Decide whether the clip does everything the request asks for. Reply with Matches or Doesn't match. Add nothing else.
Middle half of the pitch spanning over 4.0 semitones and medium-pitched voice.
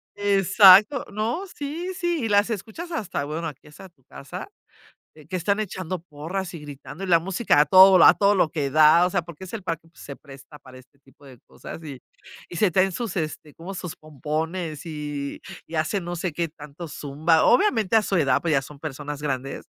Matches